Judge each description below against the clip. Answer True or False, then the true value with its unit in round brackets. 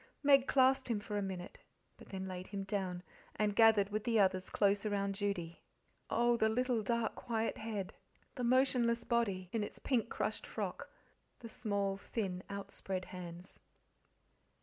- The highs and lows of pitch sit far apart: False (3.3 semitones)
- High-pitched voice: True (205 Hz)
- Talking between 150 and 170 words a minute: True (155 wpm)